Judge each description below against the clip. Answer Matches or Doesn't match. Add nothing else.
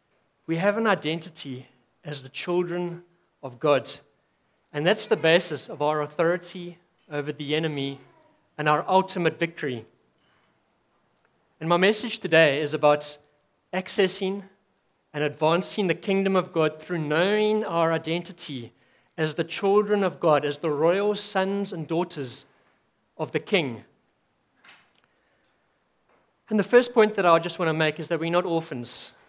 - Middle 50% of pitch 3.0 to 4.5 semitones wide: Matches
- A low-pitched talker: Doesn't match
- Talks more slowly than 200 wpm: Matches